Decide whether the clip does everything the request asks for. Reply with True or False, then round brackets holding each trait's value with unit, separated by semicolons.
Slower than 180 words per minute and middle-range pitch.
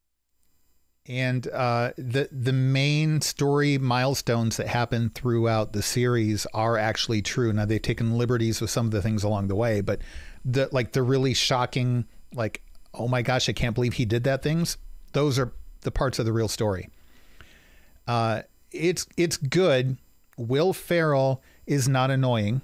False (160 wpm; 120 Hz)